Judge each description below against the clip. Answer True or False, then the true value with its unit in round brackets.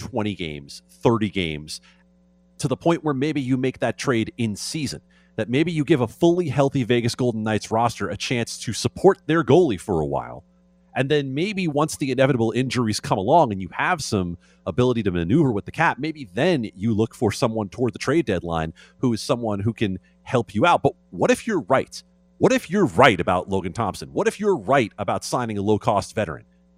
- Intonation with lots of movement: True (6.8 semitones)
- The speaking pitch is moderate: False (110 Hz)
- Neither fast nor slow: False (210 wpm)